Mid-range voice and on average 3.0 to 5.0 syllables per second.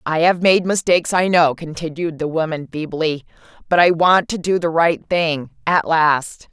Yes: medium, 165 Hz; 4.6 syllables/s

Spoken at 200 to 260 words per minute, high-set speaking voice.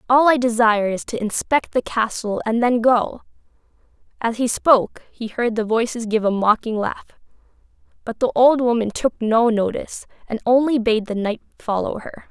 No: average, 175 wpm; high, 230 Hz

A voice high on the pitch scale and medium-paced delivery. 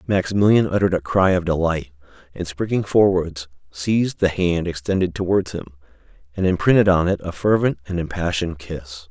No: very low, 90 Hz; average, 160 wpm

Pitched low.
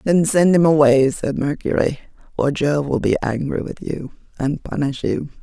No: medium, 145 Hz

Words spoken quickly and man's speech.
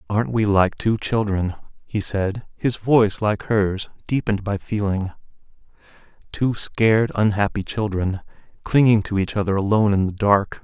No: average, 145 wpm; male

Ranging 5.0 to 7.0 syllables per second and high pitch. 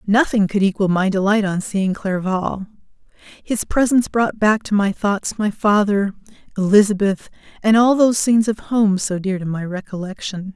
No: 4.8 syllables/s; high, 205 Hz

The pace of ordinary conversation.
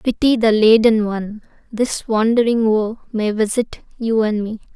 Yes: average, 150 wpm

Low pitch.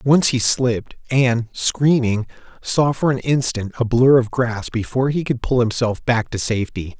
Yes: low, 120 Hz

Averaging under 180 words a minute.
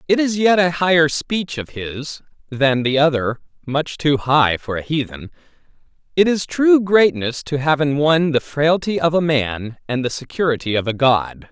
No: average, 190 wpm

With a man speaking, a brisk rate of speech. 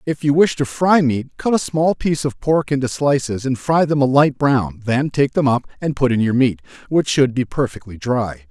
Yes: male; fast, 240 wpm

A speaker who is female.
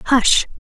Yes: female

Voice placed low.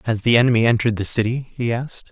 Yes: low, 115 Hz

